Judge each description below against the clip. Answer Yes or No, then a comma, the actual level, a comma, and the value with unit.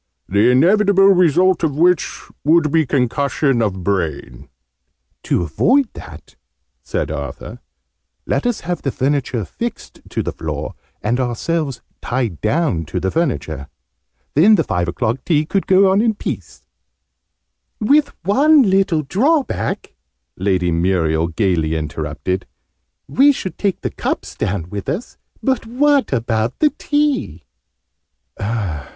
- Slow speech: Yes, slow, 130 wpm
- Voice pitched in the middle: Yes, medium, 145 Hz